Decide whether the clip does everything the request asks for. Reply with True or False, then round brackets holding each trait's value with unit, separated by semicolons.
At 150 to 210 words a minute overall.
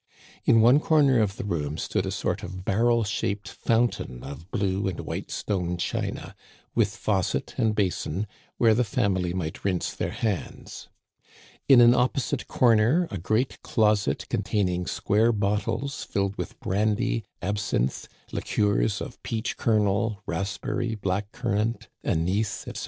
False (140 wpm)